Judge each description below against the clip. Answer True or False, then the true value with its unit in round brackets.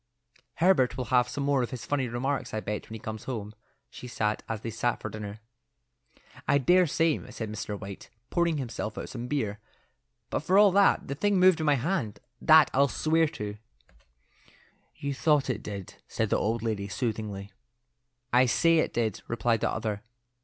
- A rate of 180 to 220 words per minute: True (185 wpm)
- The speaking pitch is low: True (120 Hz)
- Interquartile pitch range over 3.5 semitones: True (5.3 semitones)